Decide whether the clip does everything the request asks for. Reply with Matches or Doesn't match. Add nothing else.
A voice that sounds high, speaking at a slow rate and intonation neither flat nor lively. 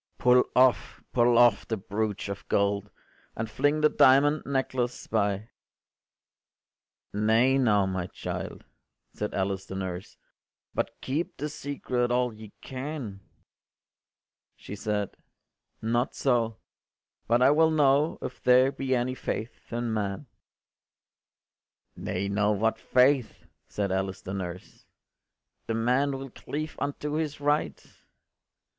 Doesn't match